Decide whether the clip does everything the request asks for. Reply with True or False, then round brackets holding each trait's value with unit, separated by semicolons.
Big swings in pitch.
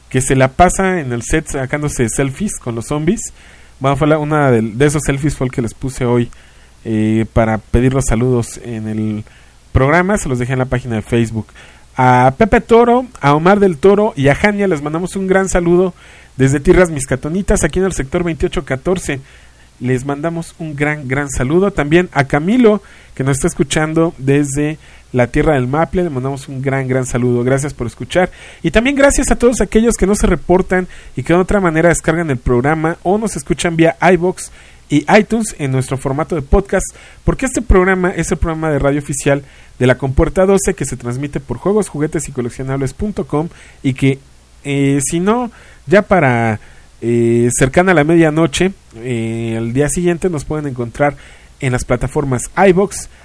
True (5.9 semitones)